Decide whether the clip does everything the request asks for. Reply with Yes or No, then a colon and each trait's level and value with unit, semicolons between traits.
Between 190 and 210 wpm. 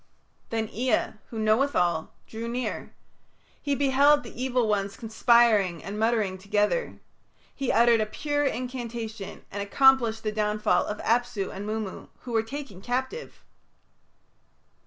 No: slow, 135 wpm